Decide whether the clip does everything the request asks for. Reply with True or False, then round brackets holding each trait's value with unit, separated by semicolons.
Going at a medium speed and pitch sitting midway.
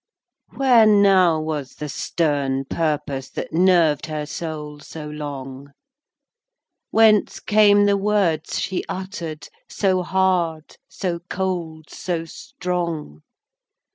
False (105 wpm; 165 Hz)